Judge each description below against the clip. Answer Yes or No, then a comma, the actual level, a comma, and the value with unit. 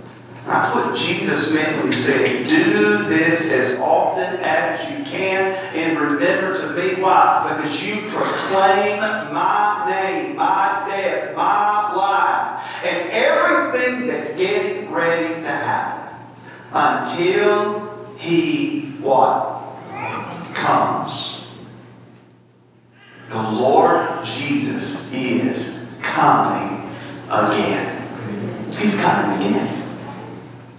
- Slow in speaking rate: Yes, slow, 95 wpm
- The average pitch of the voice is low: No, high, 190 Hz